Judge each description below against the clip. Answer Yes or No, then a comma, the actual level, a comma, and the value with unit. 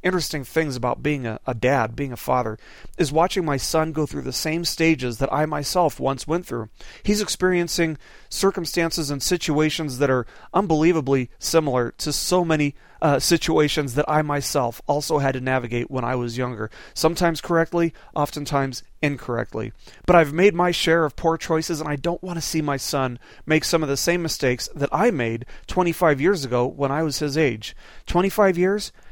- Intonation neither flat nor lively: Yes, average, 4.0 semitones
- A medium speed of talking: Yes, average, 185 wpm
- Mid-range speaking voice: Yes, medium, 150 Hz